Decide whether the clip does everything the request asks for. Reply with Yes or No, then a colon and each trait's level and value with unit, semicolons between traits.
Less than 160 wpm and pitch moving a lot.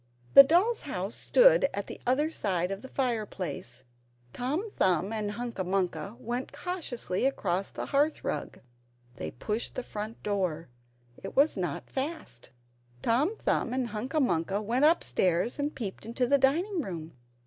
Yes: average, 150 wpm; wide, 6.8 semitones